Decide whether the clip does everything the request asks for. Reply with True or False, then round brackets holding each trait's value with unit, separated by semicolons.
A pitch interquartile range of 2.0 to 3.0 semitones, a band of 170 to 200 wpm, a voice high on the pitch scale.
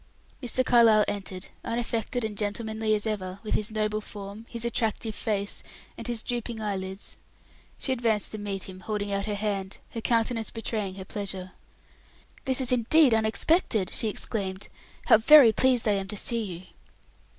False (2.5 semitones; 160 wpm; 215 Hz)